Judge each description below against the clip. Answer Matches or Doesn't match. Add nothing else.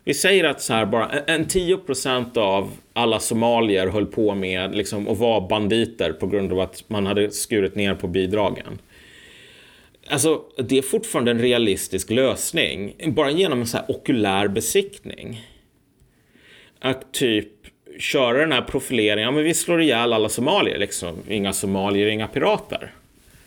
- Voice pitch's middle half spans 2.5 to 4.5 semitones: Doesn't match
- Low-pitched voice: Matches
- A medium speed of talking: Matches